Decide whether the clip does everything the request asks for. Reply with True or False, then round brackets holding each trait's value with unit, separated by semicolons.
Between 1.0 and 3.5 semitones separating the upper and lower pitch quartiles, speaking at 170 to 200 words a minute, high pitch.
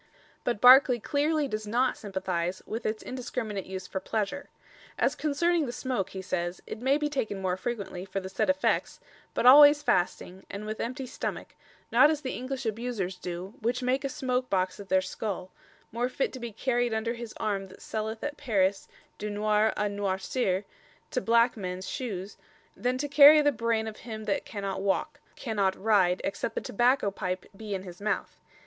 False (4.8 semitones; 190 wpm; 220 Hz)